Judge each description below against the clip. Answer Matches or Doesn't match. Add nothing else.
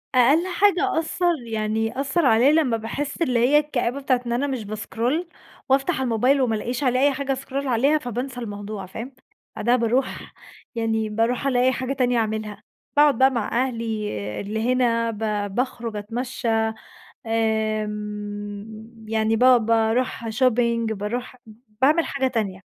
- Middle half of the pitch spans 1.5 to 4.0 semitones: Matches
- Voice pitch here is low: Doesn't match